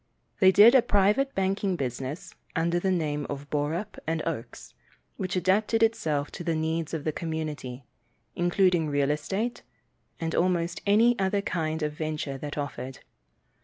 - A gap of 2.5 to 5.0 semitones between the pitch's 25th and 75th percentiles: Yes, average, 4.4 semitones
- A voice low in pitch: No, medium, 165 Hz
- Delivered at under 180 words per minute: Yes, average, 150 wpm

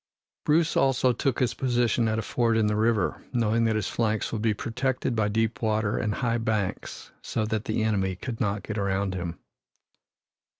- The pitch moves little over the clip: Yes, narrow, 2.0 semitones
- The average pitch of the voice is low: Yes, low, 110 Hz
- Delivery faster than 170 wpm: Yes, average, 185 wpm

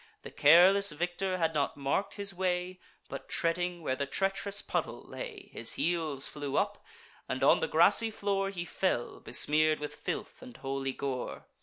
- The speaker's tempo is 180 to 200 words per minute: No, average, 165 wpm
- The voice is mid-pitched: Yes, medium, 175 Hz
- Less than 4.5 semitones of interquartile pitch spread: No, average, 5.1 semitones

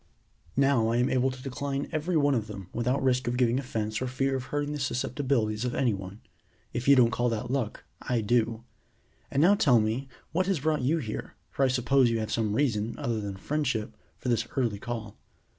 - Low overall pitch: Yes, low, 125 Hz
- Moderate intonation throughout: Yes, average, 3.5 semitones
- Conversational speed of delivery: No, fast, 210 wpm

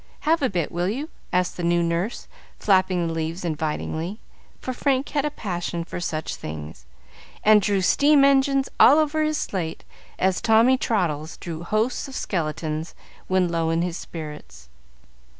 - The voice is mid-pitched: Yes, medium, 180 Hz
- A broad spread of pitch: Yes, wide, 7.4 semitones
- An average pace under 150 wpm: No, average, 160 wpm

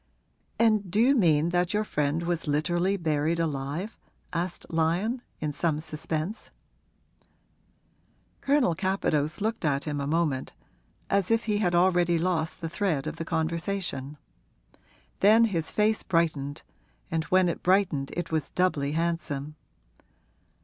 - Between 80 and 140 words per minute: Yes, slow, 135 wpm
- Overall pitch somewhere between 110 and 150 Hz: No, medium, 170 Hz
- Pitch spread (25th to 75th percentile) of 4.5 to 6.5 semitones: No, average, 3.9 semitones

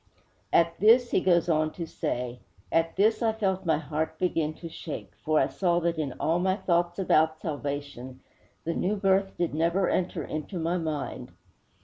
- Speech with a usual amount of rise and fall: Yes, average, 3.2 semitones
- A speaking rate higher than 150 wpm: Yes, average, 180 wpm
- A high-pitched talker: No, medium, 170 Hz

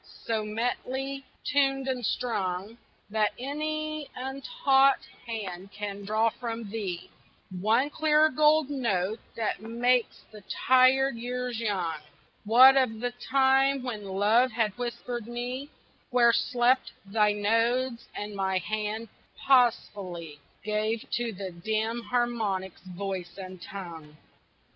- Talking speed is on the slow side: Yes, slow, 115 wpm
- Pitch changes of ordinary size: Yes, average, 4.1 semitones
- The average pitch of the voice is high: Yes, high, 230 Hz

